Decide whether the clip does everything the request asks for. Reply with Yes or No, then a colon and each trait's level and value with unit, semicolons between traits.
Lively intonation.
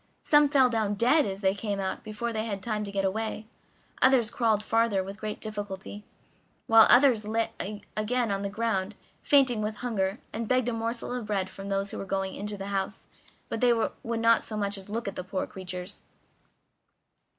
No: average, 2.7 semitones